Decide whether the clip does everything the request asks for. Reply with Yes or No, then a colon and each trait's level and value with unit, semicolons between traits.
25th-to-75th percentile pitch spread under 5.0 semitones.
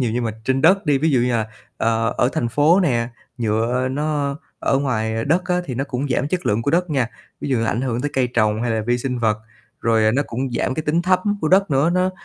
Yes: average, 4.5 semitones